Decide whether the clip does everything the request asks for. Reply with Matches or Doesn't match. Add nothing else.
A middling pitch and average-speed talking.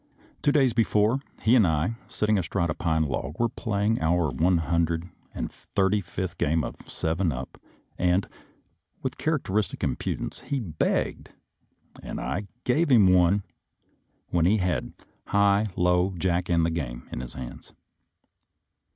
Doesn't match